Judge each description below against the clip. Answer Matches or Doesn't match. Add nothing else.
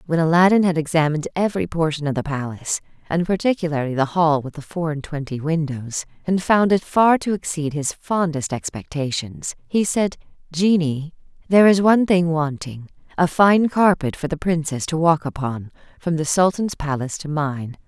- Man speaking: Doesn't match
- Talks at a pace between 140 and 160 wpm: Doesn't match